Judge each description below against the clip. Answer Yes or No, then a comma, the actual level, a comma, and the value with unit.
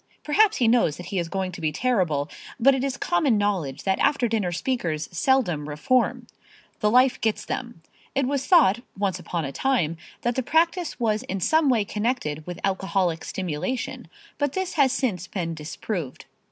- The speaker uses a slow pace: No, average, 180 wpm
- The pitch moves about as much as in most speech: No, wide, 7.2 semitones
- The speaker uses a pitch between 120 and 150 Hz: No, high, 210 Hz